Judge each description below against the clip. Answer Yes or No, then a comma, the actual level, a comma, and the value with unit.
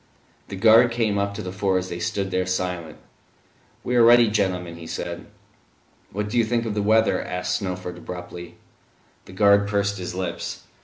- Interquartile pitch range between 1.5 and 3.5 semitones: Yes, average, 2.9 semitones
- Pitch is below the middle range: Yes, low, 100 Hz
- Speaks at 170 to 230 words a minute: Yes, average, 185 wpm